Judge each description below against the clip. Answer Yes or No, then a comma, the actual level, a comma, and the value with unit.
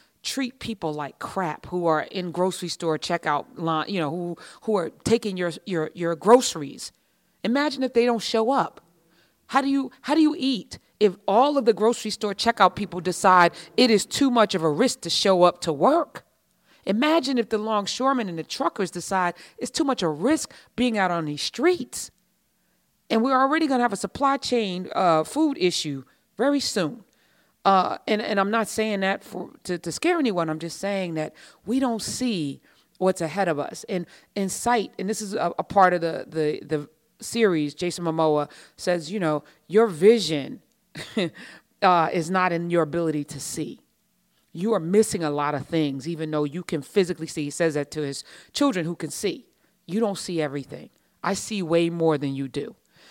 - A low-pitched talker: No, medium, 185 Hz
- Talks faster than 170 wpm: Yes, average, 195 wpm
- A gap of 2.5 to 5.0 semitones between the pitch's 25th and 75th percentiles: No, wide, 5.6 semitones